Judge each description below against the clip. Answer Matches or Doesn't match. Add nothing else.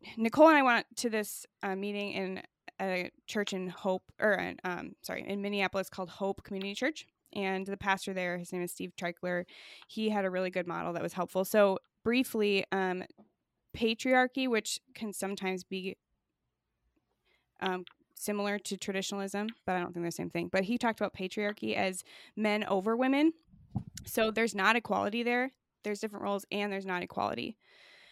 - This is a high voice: Matches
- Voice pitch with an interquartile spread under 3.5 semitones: Matches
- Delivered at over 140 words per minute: Matches